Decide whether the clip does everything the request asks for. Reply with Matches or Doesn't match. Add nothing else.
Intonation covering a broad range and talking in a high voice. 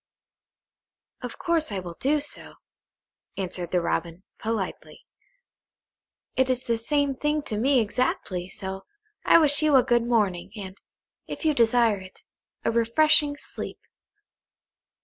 Matches